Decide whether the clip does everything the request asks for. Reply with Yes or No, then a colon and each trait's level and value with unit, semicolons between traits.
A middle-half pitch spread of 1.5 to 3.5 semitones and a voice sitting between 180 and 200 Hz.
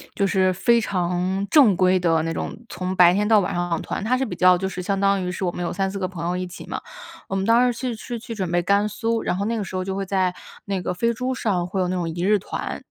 Yes: narrow, 2.4 semitones; high, 190 Hz